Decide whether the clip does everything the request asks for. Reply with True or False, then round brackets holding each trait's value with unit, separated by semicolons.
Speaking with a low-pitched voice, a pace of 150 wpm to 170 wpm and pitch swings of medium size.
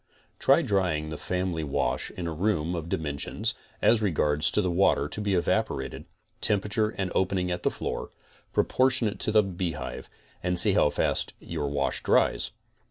True (90 Hz; 155 wpm; 4.6 semitones)